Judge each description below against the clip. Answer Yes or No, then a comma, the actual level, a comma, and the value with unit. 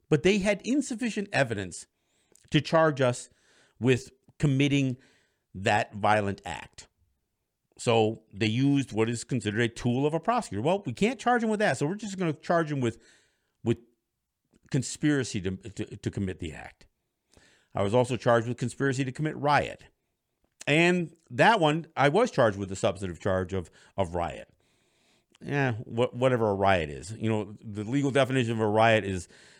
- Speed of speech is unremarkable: Yes, average, 170 wpm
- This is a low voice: Yes, low, 125 Hz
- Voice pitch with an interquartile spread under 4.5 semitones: No, wide, 5.6 semitones